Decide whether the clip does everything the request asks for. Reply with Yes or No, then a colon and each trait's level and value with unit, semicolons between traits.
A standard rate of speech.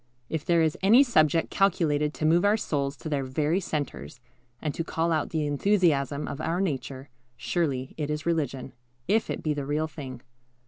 Yes: average, 185 wpm